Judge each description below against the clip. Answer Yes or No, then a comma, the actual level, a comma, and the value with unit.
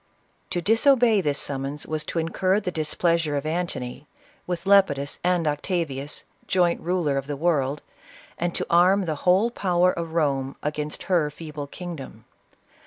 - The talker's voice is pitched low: No, medium, 165 Hz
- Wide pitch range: No, average, 3.6 semitones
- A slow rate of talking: No, average, 155 wpm